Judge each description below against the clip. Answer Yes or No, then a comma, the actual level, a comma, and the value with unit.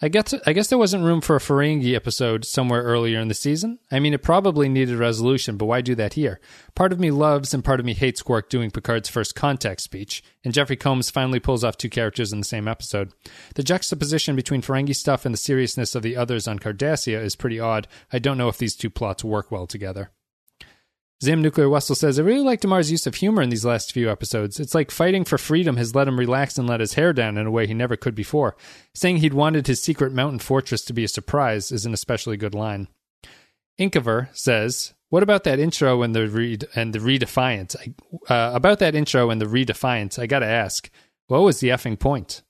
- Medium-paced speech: No, fast, 225 wpm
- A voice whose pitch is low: Yes, low, 125 Hz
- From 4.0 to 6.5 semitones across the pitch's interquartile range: Yes, average, 4.3 semitones